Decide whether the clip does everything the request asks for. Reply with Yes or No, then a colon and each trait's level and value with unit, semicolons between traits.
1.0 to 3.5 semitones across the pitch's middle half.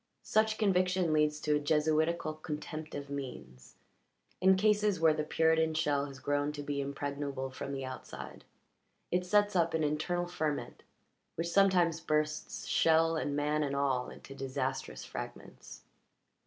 Yes: average, 3.0 semitones